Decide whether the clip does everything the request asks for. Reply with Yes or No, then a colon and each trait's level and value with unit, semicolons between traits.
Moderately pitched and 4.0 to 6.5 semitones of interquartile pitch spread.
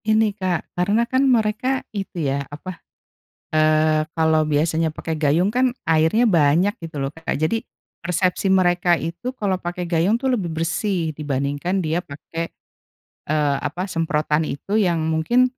Yes: medium, 170 Hz; average, 4.4 semitones